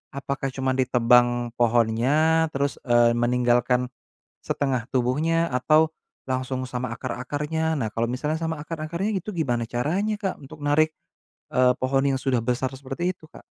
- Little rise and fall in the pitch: No, average, 4.2 semitones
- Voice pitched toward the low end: Yes, low, 130 Hz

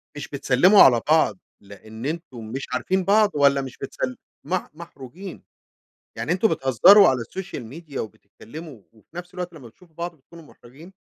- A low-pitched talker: No, medium, 145 Hz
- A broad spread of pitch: Yes, wide, 5.8 semitones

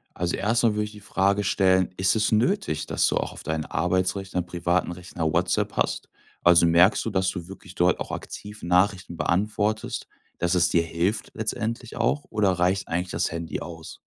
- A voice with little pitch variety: No, average, 3.3 semitones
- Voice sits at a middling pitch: No, very low, 95 Hz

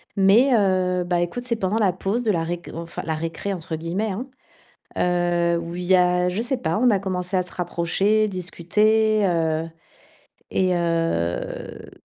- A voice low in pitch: No, medium, 180 Hz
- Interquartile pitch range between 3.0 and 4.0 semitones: Yes, average, 3.3 semitones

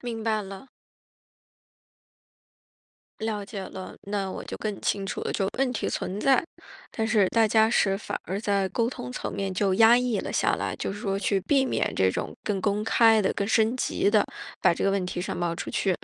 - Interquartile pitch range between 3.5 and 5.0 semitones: No, narrow, 2.5 semitones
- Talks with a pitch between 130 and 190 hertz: No, high, 205 Hz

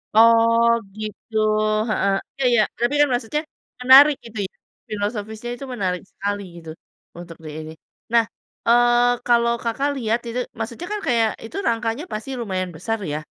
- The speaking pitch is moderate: No, high, 230 Hz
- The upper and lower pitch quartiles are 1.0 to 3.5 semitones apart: Yes, narrow, 2.5 semitones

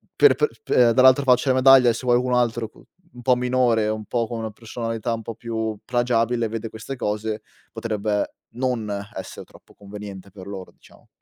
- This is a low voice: Yes, low, 115 Hz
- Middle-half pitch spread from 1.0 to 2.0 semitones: No, narrow, 2.4 semitones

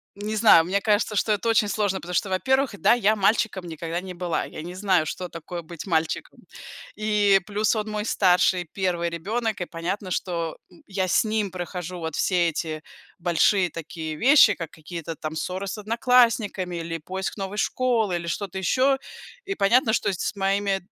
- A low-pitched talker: No, high, 190 Hz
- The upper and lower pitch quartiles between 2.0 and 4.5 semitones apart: Yes, average, 3.6 semitones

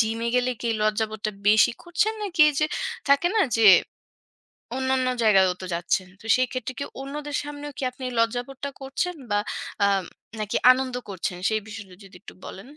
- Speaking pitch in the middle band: No, high, 245 Hz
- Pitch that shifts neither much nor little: Yes, average, 4.8 semitones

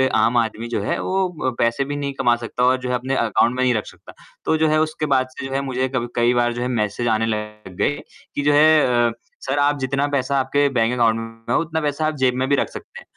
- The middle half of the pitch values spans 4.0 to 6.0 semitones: No, average, 3.3 semitones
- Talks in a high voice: No, low, 130 Hz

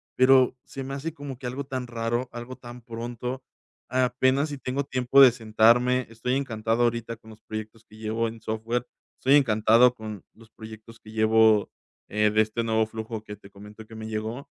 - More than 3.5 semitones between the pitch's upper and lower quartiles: No, narrow, 2.5 semitones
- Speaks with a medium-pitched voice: No, low, 115 Hz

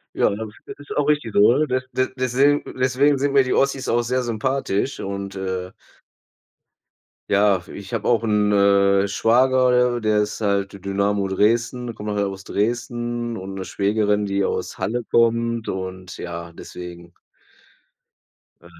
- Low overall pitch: Yes, low, 105 Hz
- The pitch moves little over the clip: No, average, 3.8 semitones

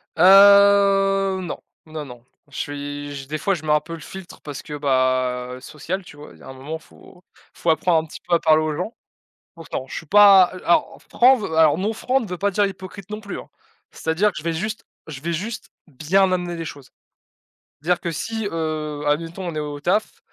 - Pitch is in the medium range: Yes, medium, 165 Hz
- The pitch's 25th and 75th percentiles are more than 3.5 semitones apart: Yes, average, 4.7 semitones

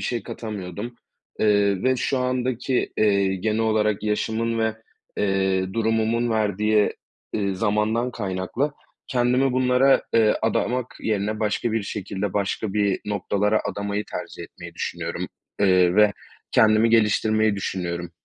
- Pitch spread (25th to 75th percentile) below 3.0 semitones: Yes, narrow, 2.4 semitones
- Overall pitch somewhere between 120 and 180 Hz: No, low, 105 Hz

